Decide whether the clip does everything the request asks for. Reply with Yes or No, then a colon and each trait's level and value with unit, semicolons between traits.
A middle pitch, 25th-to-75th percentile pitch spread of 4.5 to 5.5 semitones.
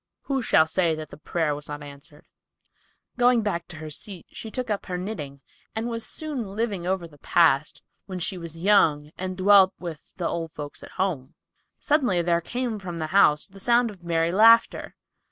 Yes: medium, 180 Hz; average, 4.9 semitones